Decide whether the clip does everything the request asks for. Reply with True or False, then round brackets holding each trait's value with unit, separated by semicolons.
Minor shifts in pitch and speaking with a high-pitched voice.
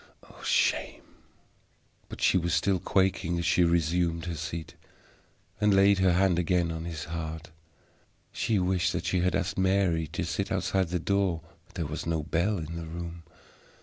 False (2.3 semitones; 85 Hz)